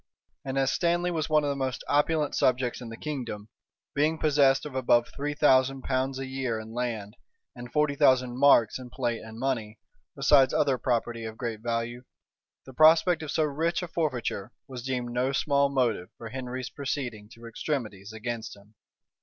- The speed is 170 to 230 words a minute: Yes, average, 180 wpm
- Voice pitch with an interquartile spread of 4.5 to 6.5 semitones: No, average, 3.4 semitones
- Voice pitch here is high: No, low, 130 Hz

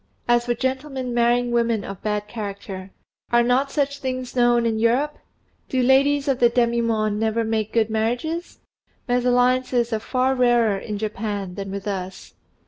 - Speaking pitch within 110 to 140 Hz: No, high, 235 Hz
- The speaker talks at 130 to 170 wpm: Yes, average, 160 wpm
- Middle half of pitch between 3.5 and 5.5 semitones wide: No, average, 2.8 semitones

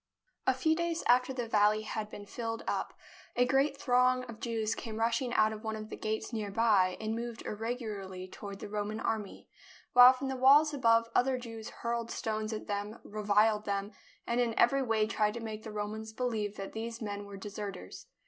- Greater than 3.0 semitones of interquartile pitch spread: No, narrow, 2.5 semitones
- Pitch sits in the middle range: No, high, 220 Hz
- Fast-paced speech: No, average, 195 wpm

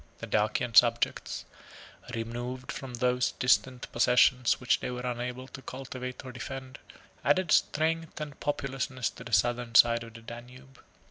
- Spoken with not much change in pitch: Yes, narrow, 1.7 semitones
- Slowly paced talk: No, average, 145 wpm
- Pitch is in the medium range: No, low, 125 Hz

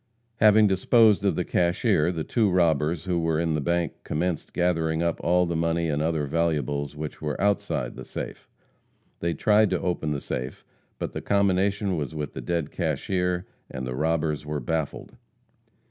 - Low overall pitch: Yes, very low, 85 Hz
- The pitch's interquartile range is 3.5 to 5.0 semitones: No, average, 3.0 semitones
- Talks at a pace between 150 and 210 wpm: Yes, average, 175 wpm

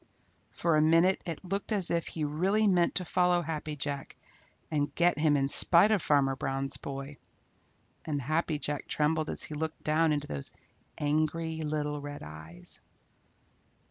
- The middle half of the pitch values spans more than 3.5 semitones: No, average, 2.7 semitones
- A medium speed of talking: Yes, average, 160 wpm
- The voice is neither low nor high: Yes, medium, 155 Hz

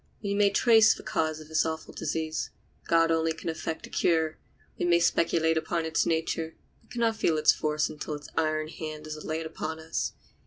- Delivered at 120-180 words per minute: No, average, 200 wpm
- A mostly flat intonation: Yes, narrow, 1.1 semitones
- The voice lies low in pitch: No, medium, 160 Hz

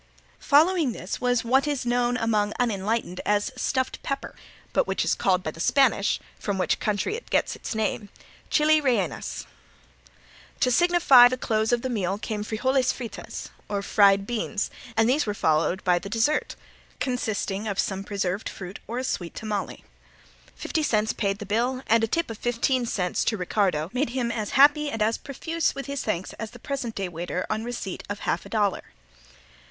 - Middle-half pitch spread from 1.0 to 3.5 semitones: No, average, 4.2 semitones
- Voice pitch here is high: Yes, high, 225 Hz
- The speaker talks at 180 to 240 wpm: Yes, average, 185 wpm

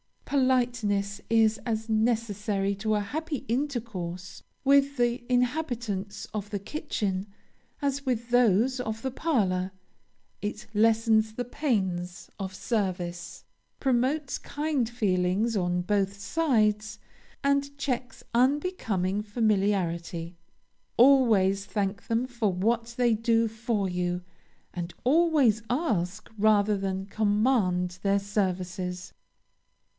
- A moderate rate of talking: No, slow, 105 wpm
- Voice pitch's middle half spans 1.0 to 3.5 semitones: No, average, 4.2 semitones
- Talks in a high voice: Yes, high, 215 Hz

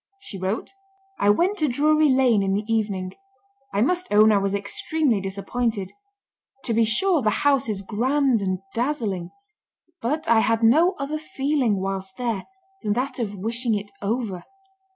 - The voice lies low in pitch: No, high, 225 Hz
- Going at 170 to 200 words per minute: No, average, 160 wpm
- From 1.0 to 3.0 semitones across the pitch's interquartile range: No, wide, 5.4 semitones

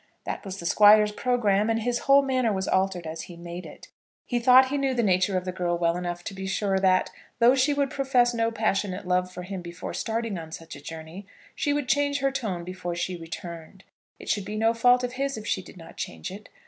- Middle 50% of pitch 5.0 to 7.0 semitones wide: Yes, wide, 5.4 semitones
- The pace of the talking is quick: Yes, fast, 235 wpm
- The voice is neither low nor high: No, high, 200 Hz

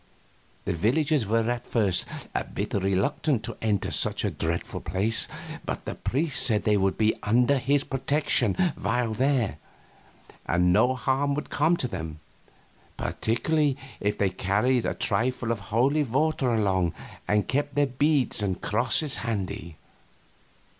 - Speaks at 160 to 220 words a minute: No, average, 145 wpm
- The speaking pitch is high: No, low, 115 Hz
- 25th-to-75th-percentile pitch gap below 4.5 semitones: No, average, 5.2 semitones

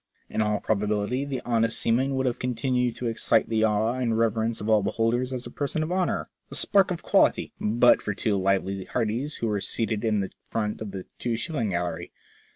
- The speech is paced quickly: Yes, fast, 210 wpm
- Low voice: Yes, low, 115 Hz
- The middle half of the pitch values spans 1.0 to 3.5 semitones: Yes, average, 3.0 semitones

